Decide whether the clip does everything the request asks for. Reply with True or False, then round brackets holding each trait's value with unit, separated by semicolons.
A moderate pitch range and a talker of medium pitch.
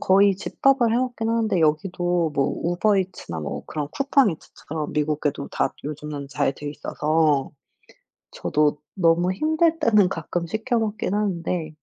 False (6.2 semitones; 175 Hz)